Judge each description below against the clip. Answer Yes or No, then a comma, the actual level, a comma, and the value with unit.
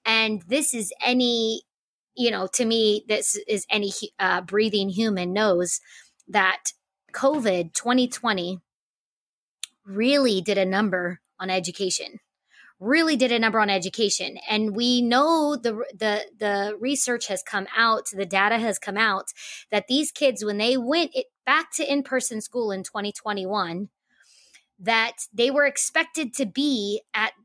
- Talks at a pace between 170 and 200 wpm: No, average, 150 wpm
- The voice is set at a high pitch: Yes, high, 220 Hz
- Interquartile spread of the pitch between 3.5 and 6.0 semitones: Yes, average, 3.9 semitones